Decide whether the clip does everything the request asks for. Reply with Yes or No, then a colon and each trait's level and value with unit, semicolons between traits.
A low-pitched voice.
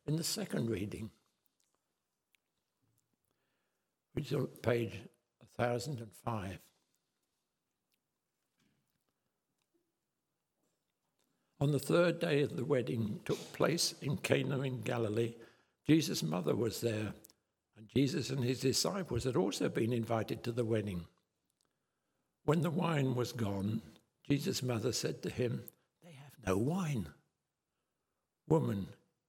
Yes: low, 120 Hz